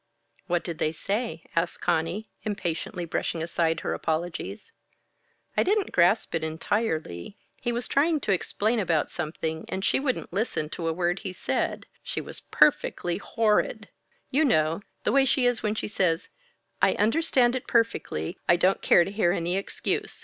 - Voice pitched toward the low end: No, medium, 185 Hz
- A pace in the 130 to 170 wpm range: Yes, average, 165 wpm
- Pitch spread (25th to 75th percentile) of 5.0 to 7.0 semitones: Yes, wide, 5.5 semitones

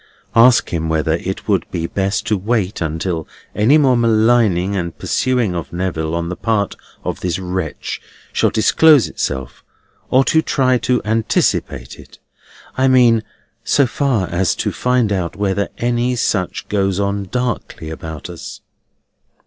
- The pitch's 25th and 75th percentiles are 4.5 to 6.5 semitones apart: Yes, wide, 5.6 semitones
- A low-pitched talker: Yes, low, 100 Hz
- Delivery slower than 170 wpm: Yes, average, 150 wpm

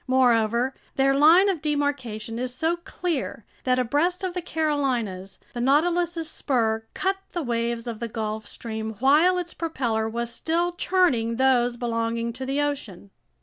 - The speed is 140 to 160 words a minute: Yes, average, 150 wpm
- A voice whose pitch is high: Yes, very high, 260 Hz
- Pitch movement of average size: No, wide, 5.7 semitones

